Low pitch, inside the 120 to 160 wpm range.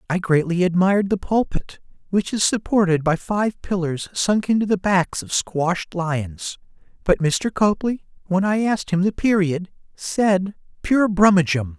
No: medium, 185 Hz; average, 155 wpm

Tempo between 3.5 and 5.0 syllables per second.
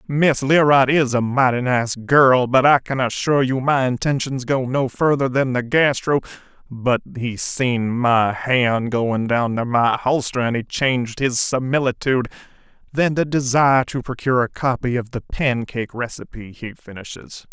Yes: 4.5 syllables/s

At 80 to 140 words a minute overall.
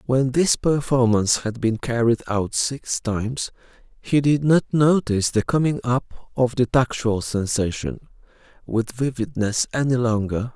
Yes: slow, 135 wpm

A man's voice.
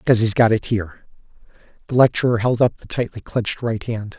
Yes: male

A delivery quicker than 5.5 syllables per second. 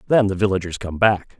Yes: 5.9 syllables/s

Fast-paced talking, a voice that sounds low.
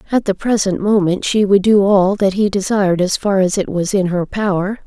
No: fast, 235 wpm; high, 195 Hz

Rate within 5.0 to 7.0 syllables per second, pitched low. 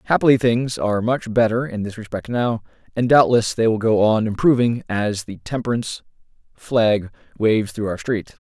Yes: 5.1 syllables/s; low, 115 Hz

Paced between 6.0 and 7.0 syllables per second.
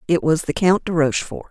Yes: 6.2 syllables/s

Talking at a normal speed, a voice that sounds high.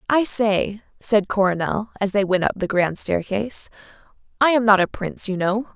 Yes: average, 190 wpm; high, 205 Hz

